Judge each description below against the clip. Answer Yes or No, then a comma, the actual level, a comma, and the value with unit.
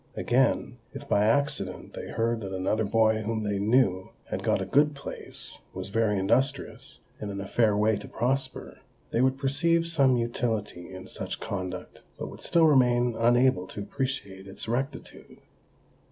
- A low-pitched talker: Yes, low, 115 Hz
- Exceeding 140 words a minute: Yes, average, 165 wpm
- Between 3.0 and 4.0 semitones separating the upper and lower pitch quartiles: No, average, 4.5 semitones